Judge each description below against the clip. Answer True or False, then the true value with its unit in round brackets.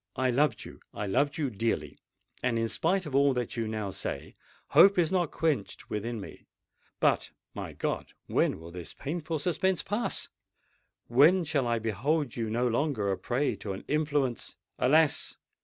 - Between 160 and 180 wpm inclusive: True (165 wpm)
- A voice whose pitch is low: True (130 Hz)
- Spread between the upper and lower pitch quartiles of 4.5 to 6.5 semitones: True (5.6 semitones)